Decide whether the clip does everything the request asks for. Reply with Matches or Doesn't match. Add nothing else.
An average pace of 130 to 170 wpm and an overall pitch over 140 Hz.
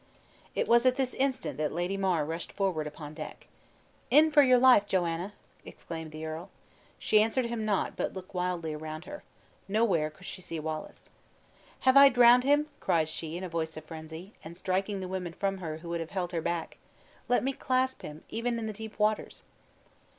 Doesn't match